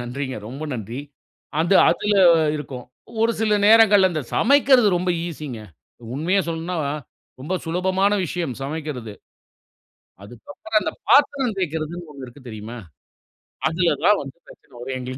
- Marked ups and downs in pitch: Yes, wide, 6.9 semitones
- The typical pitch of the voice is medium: Yes, medium, 160 Hz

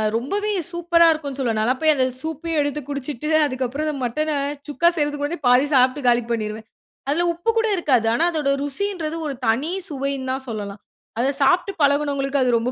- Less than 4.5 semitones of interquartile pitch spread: Yes, average, 3.6 semitones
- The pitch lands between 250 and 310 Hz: Yes, very high, 280 Hz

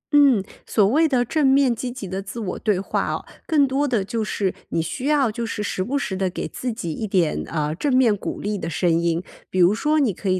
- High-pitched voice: Yes, high, 215 Hz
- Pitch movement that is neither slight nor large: No, wide, 5.8 semitones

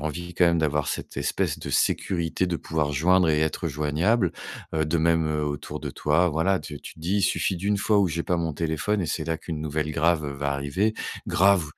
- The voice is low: Yes, very low, 80 Hz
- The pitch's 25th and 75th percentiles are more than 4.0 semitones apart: No, average, 2.9 semitones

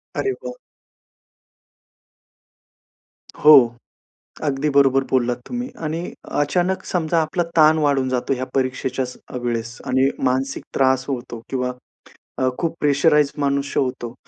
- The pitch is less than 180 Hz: Yes, low, 135 Hz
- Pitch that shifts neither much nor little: Yes, average, 3.0 semitones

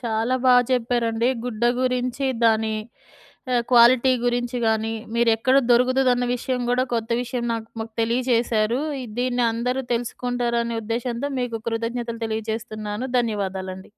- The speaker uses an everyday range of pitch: No, narrow, 1.8 semitones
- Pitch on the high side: Yes, high, 235 Hz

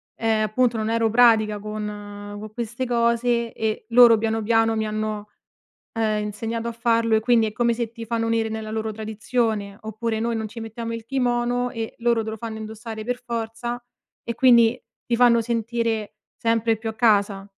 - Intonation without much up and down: Yes, narrow, 1.4 semitones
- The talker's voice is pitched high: Yes, high, 225 Hz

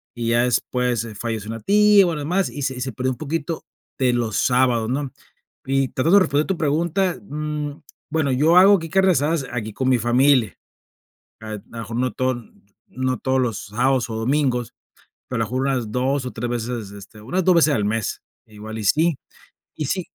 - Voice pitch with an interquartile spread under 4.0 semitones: No, average, 4.5 semitones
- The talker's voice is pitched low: Yes, low, 130 Hz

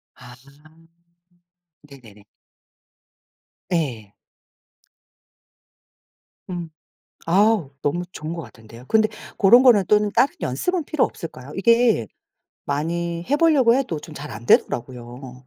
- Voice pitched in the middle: Yes, medium, 165 Hz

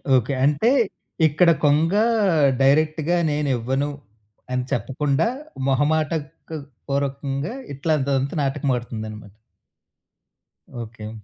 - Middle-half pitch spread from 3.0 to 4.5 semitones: No, narrow, 2.5 semitones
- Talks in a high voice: No, medium, 140 Hz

